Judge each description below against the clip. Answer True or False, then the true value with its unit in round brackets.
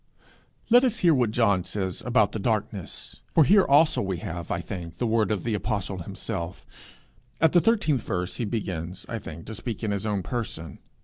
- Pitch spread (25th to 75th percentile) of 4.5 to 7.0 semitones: True (4.8 semitones)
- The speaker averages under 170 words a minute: False (195 wpm)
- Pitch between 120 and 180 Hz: False (105 Hz)